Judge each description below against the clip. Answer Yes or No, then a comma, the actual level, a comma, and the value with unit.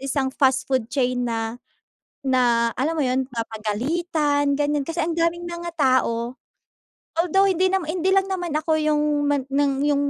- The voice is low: No, very high, 290 Hz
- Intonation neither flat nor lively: Yes, average, 4.6 semitones